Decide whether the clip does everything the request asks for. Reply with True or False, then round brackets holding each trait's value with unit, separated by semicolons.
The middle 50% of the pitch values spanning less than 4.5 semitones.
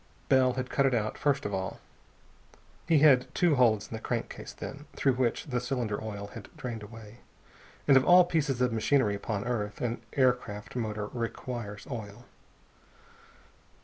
True (3.7 semitones)